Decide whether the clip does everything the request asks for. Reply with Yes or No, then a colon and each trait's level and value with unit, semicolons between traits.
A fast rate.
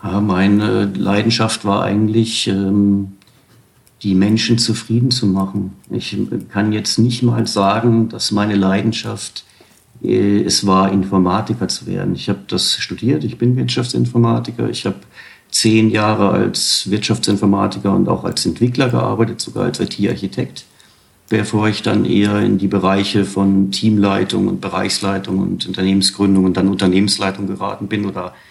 No: average, 135 wpm